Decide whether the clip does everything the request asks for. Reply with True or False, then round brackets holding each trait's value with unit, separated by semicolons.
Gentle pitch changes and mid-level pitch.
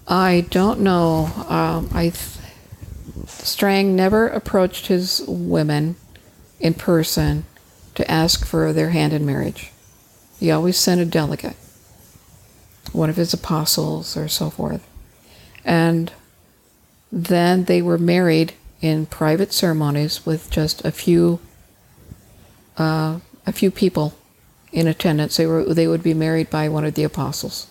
False (4.2 semitones; 160 Hz)